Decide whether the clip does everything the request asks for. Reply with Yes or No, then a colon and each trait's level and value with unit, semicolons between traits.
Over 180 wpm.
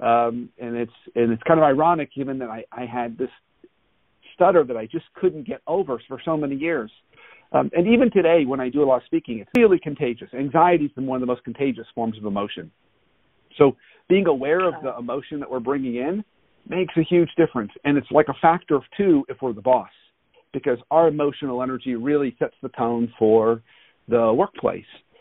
Yes: average, 200 wpm